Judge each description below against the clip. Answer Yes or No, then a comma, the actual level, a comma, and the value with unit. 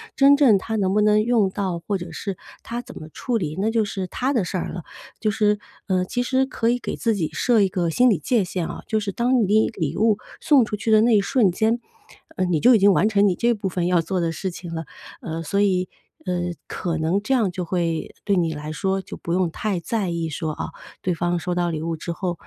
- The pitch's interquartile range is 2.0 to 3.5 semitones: No, average, 4.1 semitones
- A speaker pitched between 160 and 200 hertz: Yes, high, 190 Hz